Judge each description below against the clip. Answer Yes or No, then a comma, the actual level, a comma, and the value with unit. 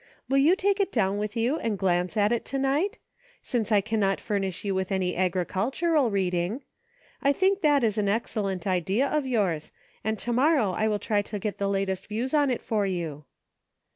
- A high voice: Yes, high, 210 Hz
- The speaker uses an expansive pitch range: Yes, wide, 5.7 semitones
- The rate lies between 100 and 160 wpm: No, average, 200 wpm